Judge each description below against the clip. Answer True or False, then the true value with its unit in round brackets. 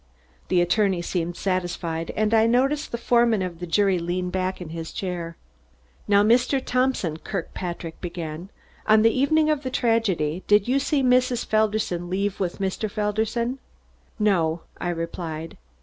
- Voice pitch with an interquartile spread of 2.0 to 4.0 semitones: False (4.9 semitones)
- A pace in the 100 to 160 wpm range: True (150 wpm)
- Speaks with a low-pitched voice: False (195 Hz)